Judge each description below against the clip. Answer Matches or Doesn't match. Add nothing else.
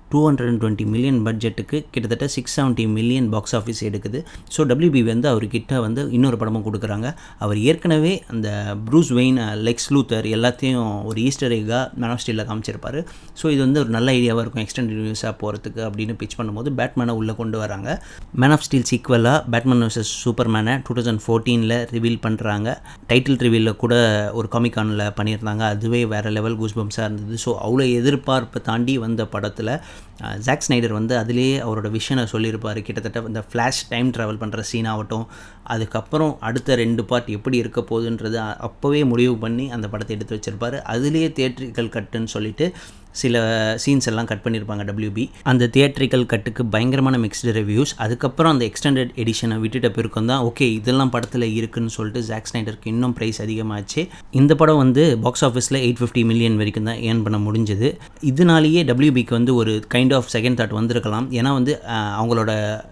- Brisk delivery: Matches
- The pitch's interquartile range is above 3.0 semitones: Doesn't match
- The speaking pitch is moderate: Doesn't match